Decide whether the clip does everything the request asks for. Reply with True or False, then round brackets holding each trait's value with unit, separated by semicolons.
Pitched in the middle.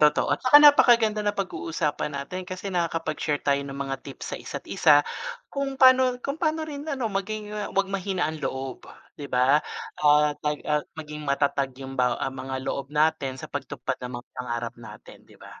True (150 Hz)